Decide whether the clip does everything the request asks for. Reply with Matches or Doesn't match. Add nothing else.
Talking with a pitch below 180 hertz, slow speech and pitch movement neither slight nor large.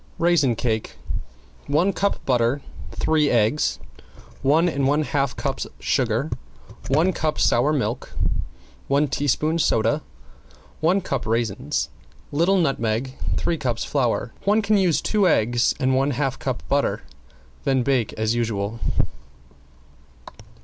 Matches